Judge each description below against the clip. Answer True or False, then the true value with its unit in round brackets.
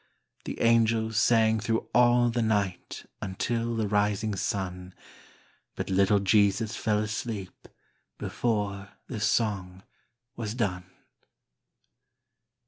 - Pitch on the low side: True (105 Hz)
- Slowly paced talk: True (100 wpm)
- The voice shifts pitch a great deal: False (2.5 semitones)